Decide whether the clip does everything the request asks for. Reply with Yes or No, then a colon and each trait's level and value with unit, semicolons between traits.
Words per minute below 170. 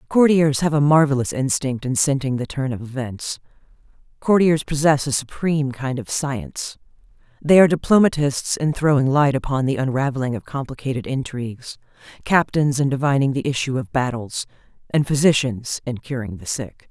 Yes: average, 155 wpm